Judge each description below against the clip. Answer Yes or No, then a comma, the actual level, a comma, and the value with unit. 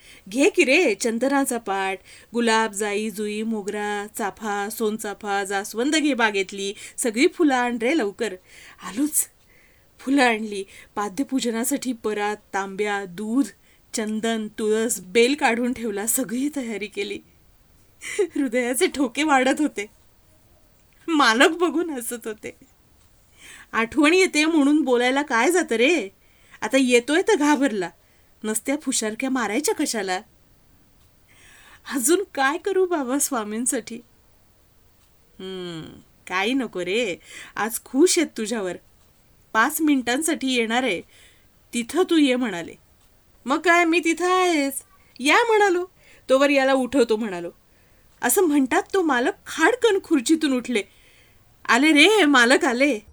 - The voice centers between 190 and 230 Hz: No, very high, 250 Hz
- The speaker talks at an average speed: Yes, average, 115 wpm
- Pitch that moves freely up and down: Yes, wide, 5.7 semitones